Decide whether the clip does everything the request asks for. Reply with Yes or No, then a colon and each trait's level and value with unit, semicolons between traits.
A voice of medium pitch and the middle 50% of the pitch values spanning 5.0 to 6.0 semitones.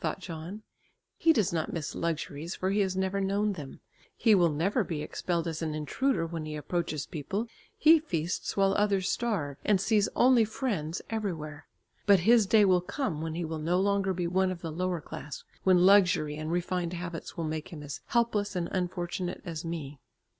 No: medium, 180 Hz; average, 3.7 semitones